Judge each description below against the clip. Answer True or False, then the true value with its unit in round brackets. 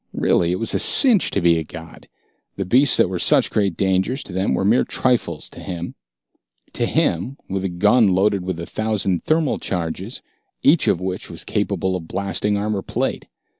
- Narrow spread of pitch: False (3.3 semitones)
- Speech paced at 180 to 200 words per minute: True (190 wpm)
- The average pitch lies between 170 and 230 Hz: False (95 Hz)